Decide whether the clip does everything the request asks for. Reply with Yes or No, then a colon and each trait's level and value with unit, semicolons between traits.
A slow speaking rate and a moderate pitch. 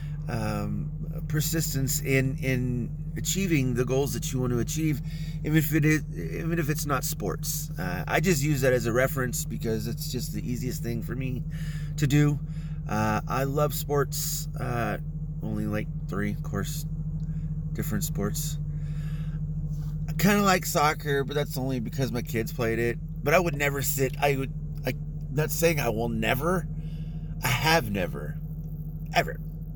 No: average, 165 wpm; medium, 155 Hz